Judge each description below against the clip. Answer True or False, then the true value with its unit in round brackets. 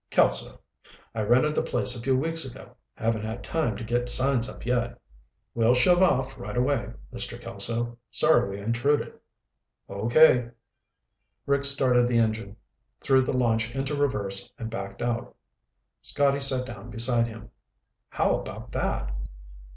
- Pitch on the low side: True (120 Hz)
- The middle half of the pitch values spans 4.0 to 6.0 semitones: False (2.8 semitones)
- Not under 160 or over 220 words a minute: False (145 wpm)